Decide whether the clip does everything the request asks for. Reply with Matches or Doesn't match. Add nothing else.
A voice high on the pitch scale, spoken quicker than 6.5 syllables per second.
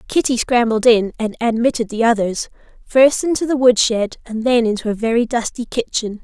Doesn't match